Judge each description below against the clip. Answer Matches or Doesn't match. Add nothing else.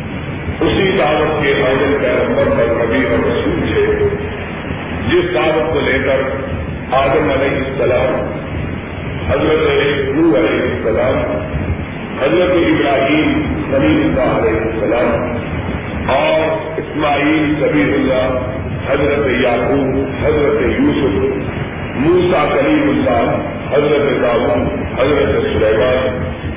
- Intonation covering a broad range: Matches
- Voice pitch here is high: Doesn't match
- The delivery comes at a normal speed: Doesn't match